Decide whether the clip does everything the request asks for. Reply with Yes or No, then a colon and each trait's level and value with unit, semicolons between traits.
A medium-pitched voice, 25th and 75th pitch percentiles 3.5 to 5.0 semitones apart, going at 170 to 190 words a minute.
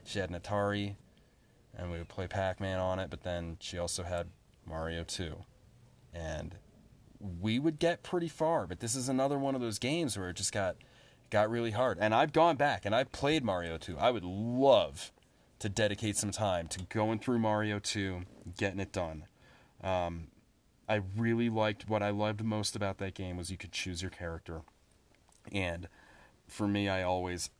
No: low, 100 Hz; average, 4.2 semitones; average, 185 wpm